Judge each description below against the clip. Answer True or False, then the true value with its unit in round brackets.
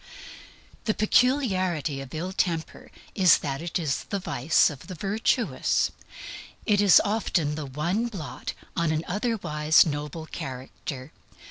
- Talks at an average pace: False (130 wpm)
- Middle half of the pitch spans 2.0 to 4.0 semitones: False (5.2 semitones)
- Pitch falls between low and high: True (170 Hz)